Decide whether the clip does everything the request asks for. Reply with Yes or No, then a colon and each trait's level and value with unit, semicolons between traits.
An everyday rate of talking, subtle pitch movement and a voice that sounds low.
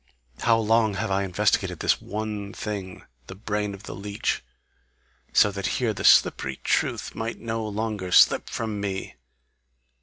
Yes: average, 150 wpm; narrow, 2.0 semitones; low, 105 Hz